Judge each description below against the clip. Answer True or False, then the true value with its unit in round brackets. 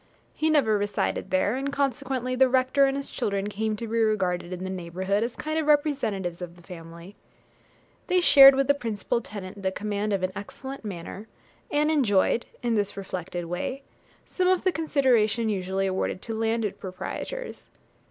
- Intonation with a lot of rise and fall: True (6.2 semitones)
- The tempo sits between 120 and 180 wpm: True (175 wpm)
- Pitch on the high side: True (215 Hz)